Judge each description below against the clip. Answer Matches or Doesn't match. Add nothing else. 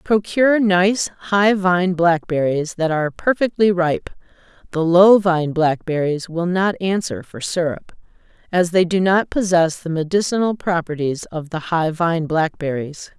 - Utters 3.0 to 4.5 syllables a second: Matches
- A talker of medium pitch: Matches